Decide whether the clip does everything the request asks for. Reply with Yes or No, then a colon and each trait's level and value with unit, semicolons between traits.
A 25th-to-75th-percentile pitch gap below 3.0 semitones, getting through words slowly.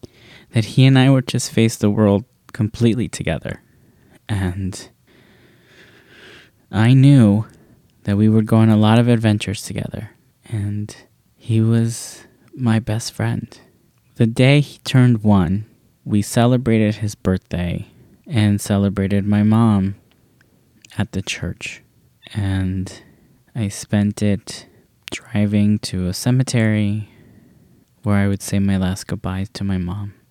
Yes: narrow, 2.6 semitones; slow, 125 wpm